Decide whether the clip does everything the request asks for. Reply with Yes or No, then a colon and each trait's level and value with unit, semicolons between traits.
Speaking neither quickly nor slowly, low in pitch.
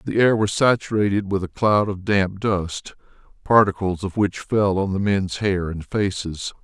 Yes: average, 180 wpm; low, 100 Hz